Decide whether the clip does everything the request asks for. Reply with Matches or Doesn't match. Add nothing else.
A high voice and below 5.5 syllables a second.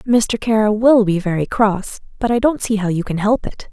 Matches